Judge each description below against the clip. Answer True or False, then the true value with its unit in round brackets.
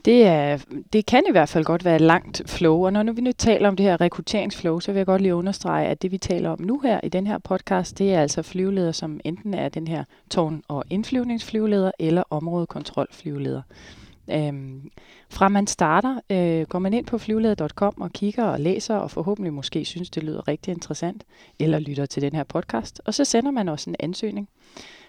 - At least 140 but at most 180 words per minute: False (205 wpm)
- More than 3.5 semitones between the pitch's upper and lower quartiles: True (4.4 semitones)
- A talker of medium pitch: True (180 Hz)